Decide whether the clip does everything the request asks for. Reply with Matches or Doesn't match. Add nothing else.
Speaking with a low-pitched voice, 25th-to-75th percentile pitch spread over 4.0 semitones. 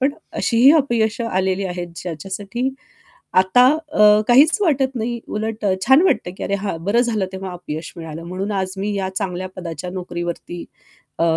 Doesn't match